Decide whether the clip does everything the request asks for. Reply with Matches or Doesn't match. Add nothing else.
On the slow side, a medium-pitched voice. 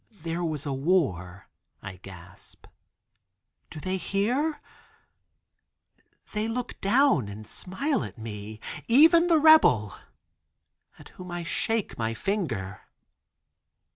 Matches